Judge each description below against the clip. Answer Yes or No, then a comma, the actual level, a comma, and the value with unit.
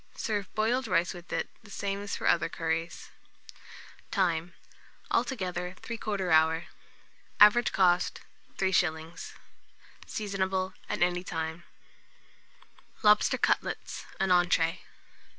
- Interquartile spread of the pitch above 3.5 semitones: No, average, 3.0 semitones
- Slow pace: Yes, slow, 100 wpm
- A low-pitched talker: No, medium, 180 Hz